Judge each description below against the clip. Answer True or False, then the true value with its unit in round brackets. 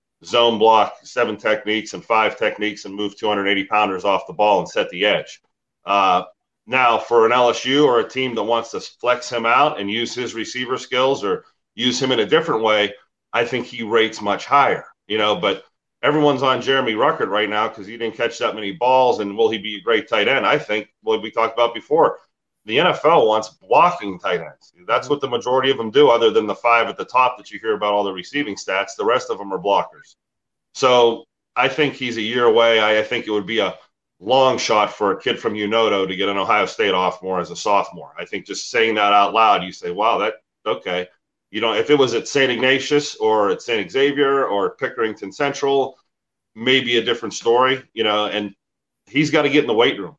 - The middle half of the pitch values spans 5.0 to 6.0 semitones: False (3.9 semitones)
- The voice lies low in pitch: True (120 Hz)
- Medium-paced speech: False (225 wpm)